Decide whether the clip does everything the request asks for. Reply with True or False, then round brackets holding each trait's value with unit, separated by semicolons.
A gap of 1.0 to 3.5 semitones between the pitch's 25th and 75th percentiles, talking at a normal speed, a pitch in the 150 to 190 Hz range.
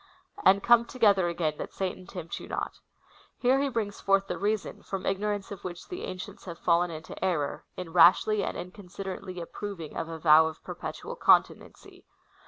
True (3.1 semitones; 175 wpm; 185 Hz)